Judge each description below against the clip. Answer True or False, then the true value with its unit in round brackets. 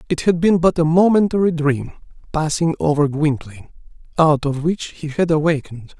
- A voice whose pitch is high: False (155 Hz)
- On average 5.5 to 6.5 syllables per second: False (5.3 syllables/s)